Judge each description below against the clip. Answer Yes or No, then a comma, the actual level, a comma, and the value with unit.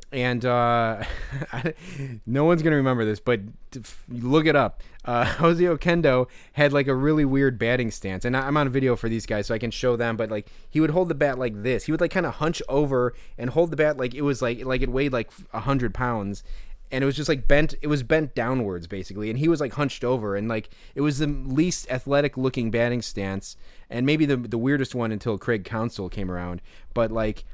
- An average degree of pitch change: Yes, average, 4.2 semitones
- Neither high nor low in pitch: No, low, 125 Hz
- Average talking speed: No, fast, 225 wpm